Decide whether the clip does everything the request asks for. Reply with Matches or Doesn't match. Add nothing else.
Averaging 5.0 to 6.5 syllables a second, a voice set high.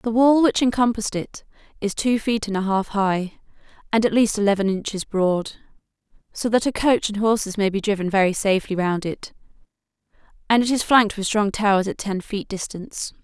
Matches